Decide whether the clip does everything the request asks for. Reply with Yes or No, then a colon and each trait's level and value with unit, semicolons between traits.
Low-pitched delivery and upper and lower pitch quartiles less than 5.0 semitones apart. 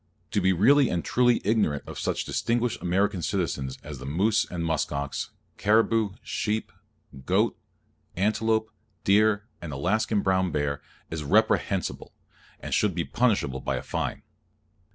No: very low, 95 Hz; average, 5.3 semitones